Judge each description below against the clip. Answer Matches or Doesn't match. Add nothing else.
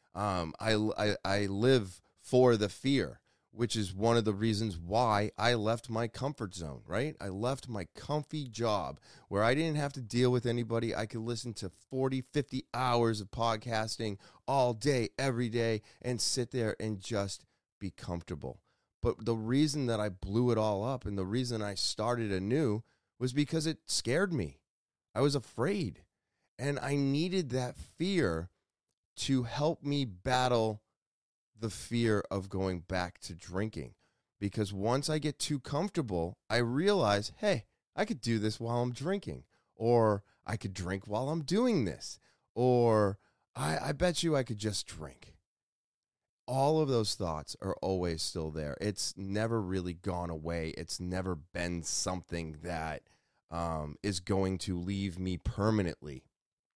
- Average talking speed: Matches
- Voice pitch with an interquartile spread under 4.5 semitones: Doesn't match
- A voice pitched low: Matches